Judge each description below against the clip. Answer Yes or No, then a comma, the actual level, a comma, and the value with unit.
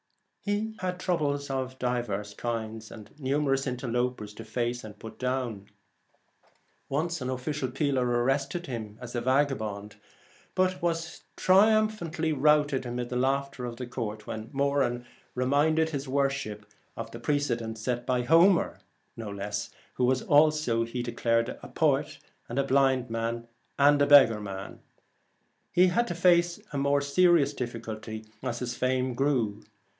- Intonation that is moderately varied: Yes, average, 3.8 semitones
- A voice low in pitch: Yes, low, 130 Hz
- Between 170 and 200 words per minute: No, average, 150 wpm